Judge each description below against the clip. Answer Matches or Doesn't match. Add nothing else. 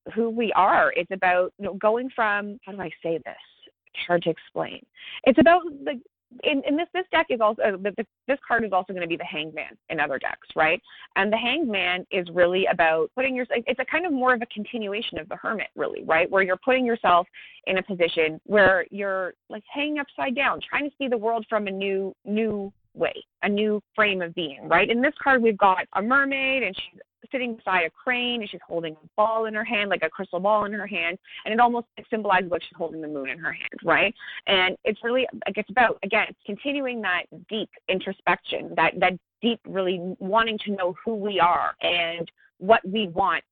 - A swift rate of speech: Matches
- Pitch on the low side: Doesn't match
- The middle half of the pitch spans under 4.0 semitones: Doesn't match